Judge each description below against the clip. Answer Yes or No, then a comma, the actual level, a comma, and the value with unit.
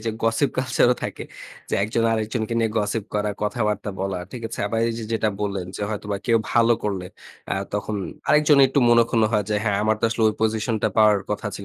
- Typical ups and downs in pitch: No, narrow, 1.9 semitones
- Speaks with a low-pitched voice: Yes, low, 110 Hz